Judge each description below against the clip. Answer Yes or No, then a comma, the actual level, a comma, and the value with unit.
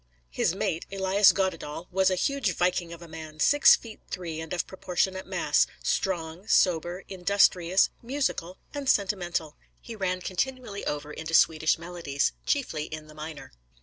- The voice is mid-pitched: Yes, medium, 180 Hz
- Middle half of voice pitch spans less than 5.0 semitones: Yes, average, 3.3 semitones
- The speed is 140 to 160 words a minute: Yes, average, 150 wpm